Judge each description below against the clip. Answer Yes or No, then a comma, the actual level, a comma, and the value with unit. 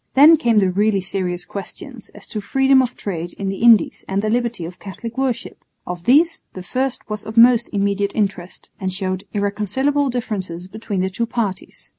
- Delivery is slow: No, average, 185 wpm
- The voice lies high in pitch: Yes, high, 210 Hz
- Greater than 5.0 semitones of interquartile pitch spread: No, average, 4.2 semitones